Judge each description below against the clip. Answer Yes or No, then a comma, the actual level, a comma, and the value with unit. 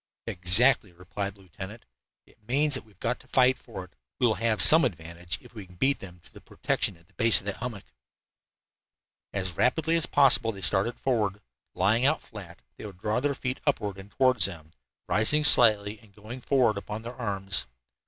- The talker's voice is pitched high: No, low, 110 Hz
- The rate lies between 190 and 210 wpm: Yes, average, 200 wpm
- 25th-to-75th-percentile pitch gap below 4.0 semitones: No, average, 4.6 semitones